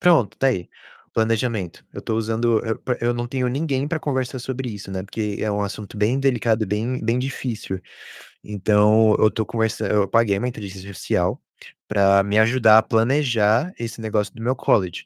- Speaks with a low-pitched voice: Yes, low, 110 Hz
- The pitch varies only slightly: No, average, 3.1 semitones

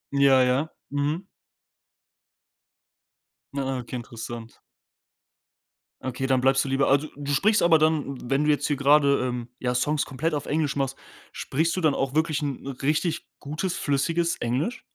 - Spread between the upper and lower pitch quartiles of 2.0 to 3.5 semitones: Yes, narrow, 2.6 semitones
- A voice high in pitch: No, medium, 140 Hz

